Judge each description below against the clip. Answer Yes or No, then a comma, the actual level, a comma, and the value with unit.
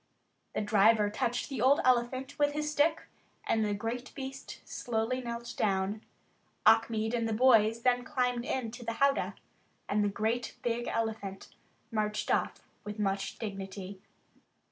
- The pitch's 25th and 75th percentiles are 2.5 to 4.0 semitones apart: Yes, average, 3.1 semitones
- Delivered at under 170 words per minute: Yes, average, 145 wpm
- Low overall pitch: No, high, 230 Hz